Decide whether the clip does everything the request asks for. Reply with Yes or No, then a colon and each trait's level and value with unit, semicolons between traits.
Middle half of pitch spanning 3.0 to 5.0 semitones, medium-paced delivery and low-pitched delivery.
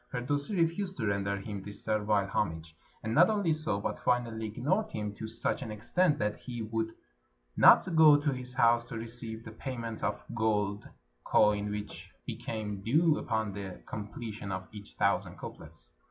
Yes: average, 3.7 semitones; average, 170 wpm; low, 110 Hz